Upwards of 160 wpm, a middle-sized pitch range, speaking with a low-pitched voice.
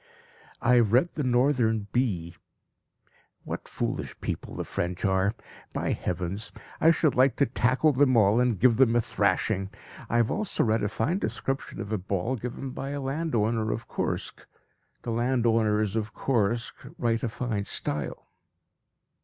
No: average, 155 wpm; average, 3.5 semitones; low, 115 Hz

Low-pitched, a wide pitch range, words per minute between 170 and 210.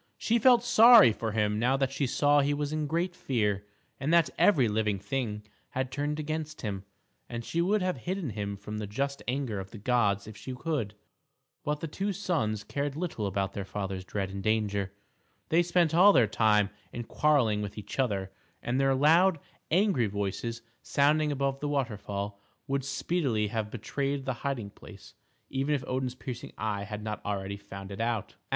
Yes: low, 125 Hz; wide, 6.1 semitones; average, 185 wpm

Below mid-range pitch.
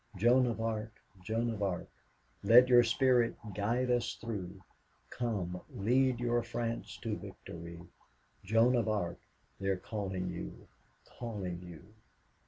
Yes: low, 110 Hz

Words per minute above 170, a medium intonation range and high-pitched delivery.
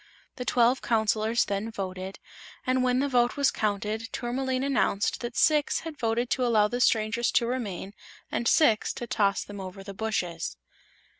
No: average, 165 wpm; average, 3.4 semitones; high, 230 Hz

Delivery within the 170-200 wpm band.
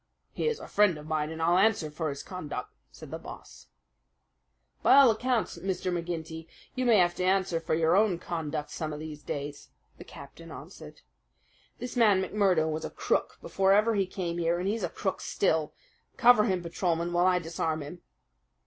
Yes: average, 190 wpm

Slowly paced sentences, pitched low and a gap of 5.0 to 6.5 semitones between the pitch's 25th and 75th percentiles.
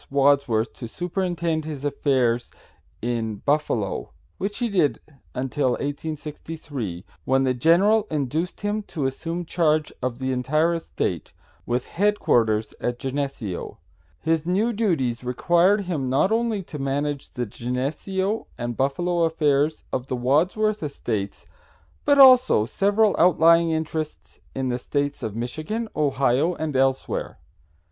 No: slow, 125 wpm; medium, 150 Hz; wide, 5.4 semitones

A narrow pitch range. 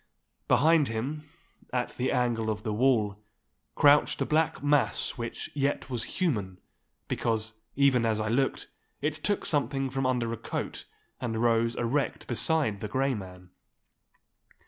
No: average, 4.2 semitones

